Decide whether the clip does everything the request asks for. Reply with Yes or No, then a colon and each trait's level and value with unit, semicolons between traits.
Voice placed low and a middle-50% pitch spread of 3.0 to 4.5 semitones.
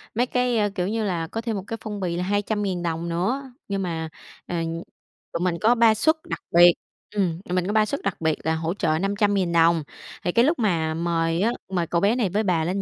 No: high, 190 Hz; average, 4.1 semitones